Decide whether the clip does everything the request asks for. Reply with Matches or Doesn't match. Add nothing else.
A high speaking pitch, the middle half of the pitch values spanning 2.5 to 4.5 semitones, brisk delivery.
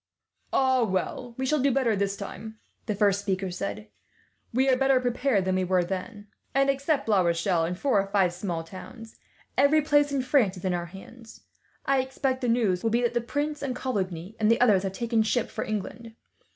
Doesn't match